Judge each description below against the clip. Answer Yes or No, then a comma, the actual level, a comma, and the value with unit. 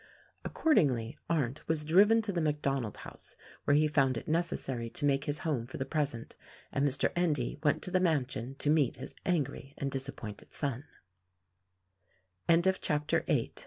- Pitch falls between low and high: Yes, medium, 145 Hz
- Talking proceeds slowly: No, average, 150 wpm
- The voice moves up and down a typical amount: Yes, average, 3.2 semitones